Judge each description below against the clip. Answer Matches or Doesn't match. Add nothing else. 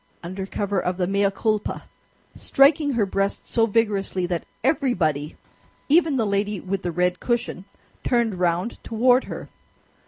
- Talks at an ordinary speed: Matches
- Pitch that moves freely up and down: Doesn't match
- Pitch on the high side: Matches